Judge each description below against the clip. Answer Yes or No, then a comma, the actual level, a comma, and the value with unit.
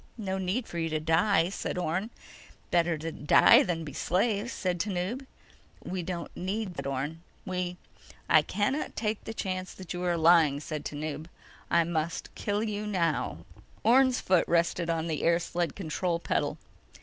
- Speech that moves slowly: No, average, 170 wpm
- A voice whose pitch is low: No, medium, 175 Hz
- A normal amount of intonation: Yes, average, 3.4 semitones